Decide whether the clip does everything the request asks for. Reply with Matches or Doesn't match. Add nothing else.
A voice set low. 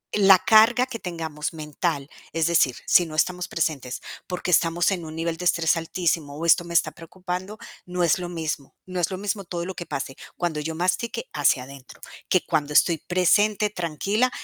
Doesn't match